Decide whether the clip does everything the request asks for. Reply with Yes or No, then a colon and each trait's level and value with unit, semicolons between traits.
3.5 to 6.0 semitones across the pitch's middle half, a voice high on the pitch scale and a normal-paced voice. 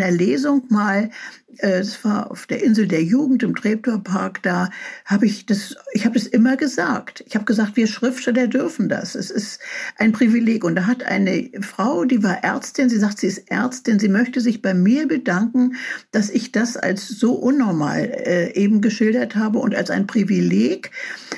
Yes: average, 3.9 semitones; high, 225 Hz; average, 175 wpm